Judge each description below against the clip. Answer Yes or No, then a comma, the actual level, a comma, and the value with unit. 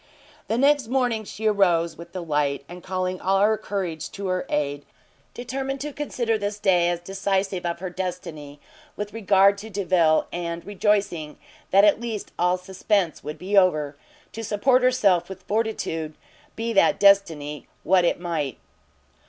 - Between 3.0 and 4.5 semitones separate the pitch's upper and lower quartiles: Yes, average, 3.5 semitones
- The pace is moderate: Yes, average, 160 wpm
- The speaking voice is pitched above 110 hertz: Yes, high, 190 Hz